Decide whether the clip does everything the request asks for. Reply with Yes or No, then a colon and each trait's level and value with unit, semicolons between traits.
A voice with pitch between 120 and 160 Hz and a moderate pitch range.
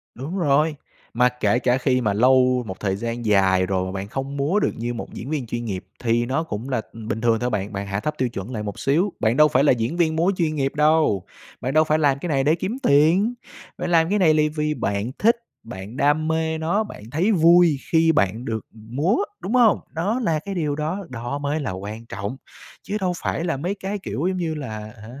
No: medium, 140 Hz; wide, 6.0 semitones